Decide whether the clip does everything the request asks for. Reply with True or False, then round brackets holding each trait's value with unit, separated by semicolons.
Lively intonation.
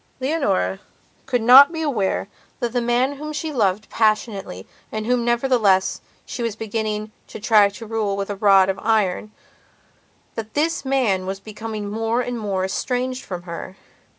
False (3.7 semitones)